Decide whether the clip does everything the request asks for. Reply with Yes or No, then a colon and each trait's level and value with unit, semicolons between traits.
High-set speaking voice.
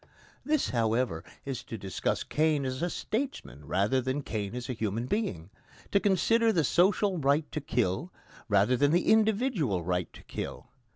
No: low, 130 Hz